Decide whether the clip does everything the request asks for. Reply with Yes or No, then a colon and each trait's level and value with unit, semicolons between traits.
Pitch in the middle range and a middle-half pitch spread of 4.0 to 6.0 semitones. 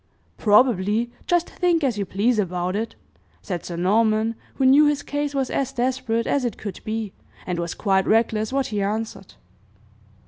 No: high, 225 Hz; average, 4.6 semitones